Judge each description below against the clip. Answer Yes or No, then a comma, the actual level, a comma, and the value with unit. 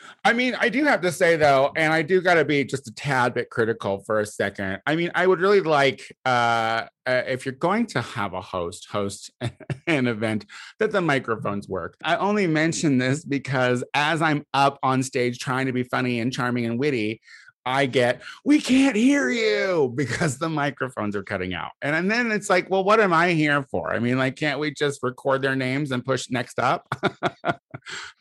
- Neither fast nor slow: No, fast, 210 wpm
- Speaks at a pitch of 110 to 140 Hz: Yes, low, 135 Hz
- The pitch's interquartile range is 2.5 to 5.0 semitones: No, wide, 5.5 semitones